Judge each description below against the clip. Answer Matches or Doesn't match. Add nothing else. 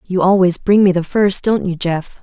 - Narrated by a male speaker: Doesn't match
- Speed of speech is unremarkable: Doesn't match